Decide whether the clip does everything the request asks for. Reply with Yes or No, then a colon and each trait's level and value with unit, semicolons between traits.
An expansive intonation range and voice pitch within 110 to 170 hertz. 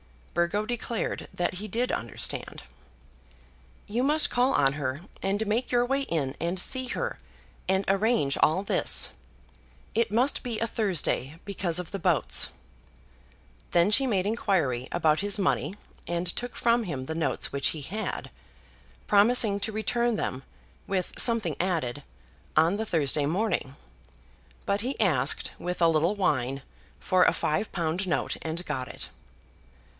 No: wide, 5.7 semitones; high, 190 Hz